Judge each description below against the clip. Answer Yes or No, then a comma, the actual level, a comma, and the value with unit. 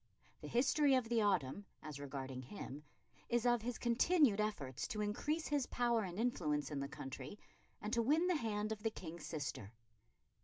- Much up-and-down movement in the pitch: Yes, wide, 8.3 semitones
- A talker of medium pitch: No, high, 210 Hz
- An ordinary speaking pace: Yes, average, 180 wpm